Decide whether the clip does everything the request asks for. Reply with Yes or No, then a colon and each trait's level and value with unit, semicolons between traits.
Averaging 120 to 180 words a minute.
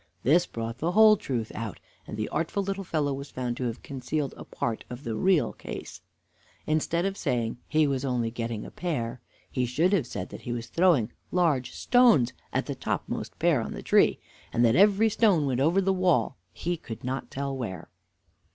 No: average, 195 wpm